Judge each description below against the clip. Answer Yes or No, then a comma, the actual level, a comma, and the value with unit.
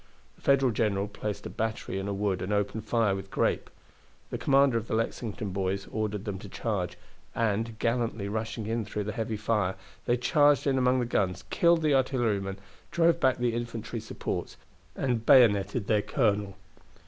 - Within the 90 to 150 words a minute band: No, average, 175 wpm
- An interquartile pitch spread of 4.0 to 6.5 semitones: No, average, 3.2 semitones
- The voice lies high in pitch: No, low, 110 Hz